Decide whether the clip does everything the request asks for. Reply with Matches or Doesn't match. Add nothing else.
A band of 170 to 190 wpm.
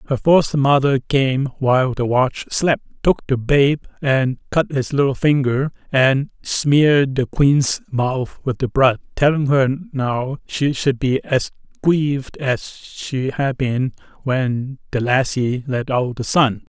Doesn't match